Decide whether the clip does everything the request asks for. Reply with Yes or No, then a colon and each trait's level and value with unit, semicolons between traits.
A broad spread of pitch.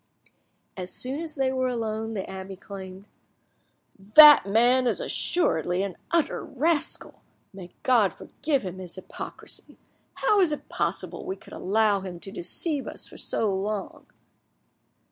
Yes: wide, 6.4 semitones